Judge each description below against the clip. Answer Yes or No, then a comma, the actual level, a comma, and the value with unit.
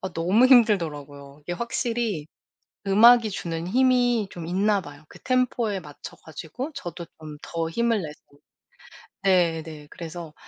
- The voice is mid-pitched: Yes, medium, 180 Hz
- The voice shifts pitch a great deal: Yes, wide, 6.4 semitones